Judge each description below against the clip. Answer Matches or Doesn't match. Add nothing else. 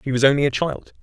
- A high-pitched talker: Doesn't match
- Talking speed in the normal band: Doesn't match